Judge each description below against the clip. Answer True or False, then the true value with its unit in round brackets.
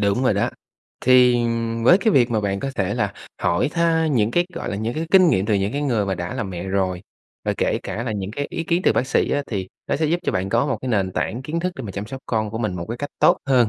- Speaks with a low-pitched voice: True (115 Hz)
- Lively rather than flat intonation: True (5.9 semitones)